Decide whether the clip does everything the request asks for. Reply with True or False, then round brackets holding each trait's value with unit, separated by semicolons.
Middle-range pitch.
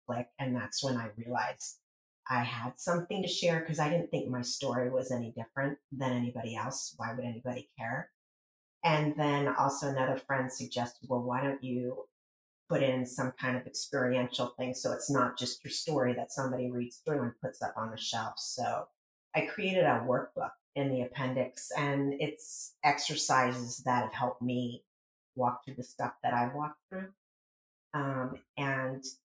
False (130 Hz)